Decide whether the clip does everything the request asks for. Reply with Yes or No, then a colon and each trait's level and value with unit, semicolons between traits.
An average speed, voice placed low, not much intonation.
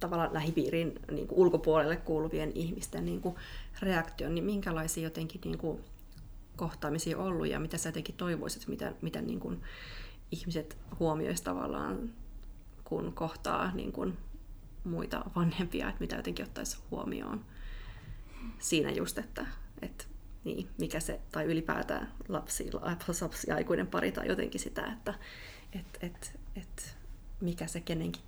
No: average, 135 wpm; medium, 165 Hz; narrow, 2.0 semitones